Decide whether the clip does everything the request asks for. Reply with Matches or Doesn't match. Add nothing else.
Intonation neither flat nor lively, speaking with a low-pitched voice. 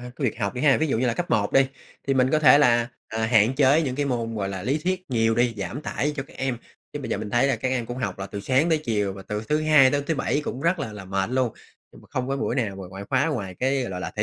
Matches